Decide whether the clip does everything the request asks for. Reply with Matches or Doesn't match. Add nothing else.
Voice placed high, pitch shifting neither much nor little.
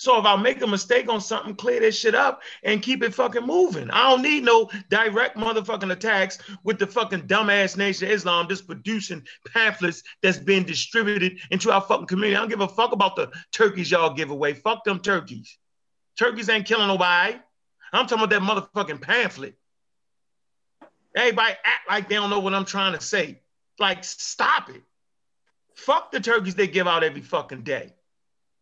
Matches